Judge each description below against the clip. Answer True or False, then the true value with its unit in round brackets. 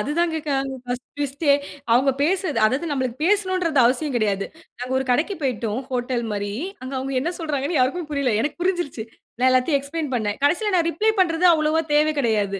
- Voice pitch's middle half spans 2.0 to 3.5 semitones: False (4.8 semitones)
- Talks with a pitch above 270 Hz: True (280 Hz)